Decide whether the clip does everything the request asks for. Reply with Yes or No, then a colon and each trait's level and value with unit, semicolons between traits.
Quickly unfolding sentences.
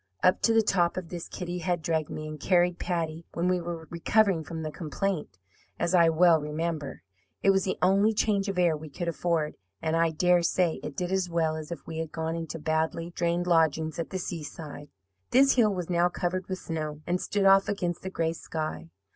Yes: fast, 215 wpm